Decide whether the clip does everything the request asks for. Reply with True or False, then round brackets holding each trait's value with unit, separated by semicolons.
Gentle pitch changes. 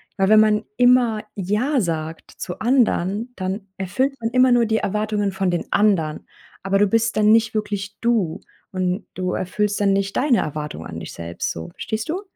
False (3.4 semitones)